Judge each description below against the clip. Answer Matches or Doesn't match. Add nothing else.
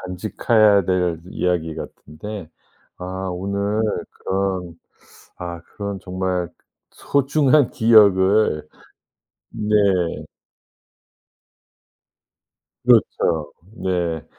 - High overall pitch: Doesn't match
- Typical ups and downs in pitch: Matches